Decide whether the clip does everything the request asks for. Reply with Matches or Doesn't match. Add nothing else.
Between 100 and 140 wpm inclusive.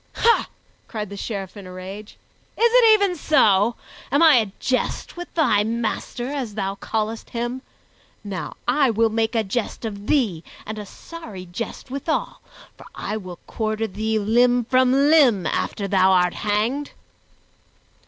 Doesn't match